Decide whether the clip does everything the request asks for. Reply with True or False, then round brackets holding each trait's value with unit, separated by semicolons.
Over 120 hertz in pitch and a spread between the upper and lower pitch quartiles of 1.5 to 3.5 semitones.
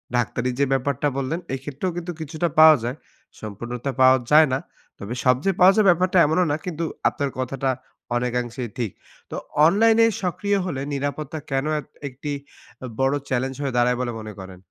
False (135 Hz; 4.5 semitones)